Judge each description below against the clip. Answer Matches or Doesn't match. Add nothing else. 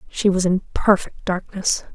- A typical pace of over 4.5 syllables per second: Doesn't match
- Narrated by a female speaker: Matches